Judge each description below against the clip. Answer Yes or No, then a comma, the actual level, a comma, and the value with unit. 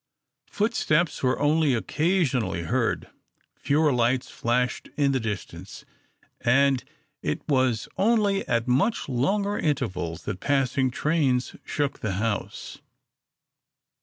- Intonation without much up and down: No, average, 4.6 semitones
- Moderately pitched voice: No, low, 130 Hz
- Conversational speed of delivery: No, slow, 105 wpm